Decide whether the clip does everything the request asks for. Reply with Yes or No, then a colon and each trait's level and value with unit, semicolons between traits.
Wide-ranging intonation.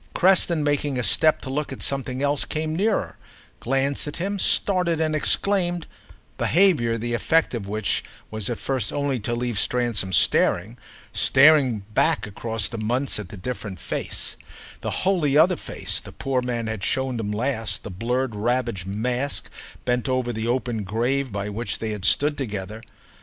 No: average, 4.8 semitones